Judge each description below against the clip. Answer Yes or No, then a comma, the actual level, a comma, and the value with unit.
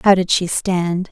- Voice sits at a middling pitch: Yes, medium, 180 Hz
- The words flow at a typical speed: No, fast, 215 wpm